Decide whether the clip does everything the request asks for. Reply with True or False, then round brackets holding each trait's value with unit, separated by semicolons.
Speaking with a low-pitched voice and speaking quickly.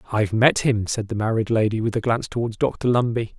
True (115 Hz; 230 wpm)